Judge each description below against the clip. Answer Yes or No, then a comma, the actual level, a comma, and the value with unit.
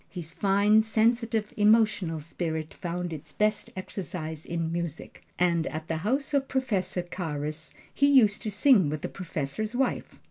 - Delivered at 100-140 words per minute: No, average, 150 wpm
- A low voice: No, medium, 185 Hz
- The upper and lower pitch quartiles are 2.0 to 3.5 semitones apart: No, average, 5.1 semitones